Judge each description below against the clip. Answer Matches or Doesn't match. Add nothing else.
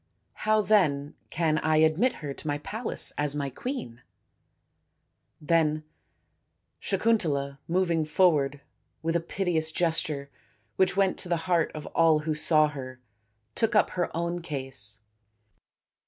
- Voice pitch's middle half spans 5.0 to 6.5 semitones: Doesn't match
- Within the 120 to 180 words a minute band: Matches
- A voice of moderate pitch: Matches